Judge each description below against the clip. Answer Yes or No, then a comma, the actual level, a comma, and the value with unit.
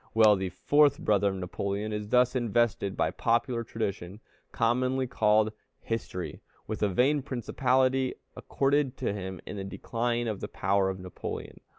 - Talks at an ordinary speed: Yes, average, 155 wpm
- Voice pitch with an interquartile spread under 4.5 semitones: Yes, average, 4.1 semitones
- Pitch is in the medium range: No, low, 110 Hz